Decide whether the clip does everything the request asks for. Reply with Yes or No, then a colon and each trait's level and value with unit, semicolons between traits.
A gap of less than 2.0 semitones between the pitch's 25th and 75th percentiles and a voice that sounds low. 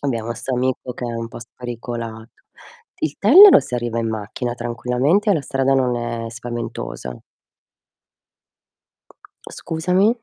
No: narrow, 2.5 semitones; low, 120 Hz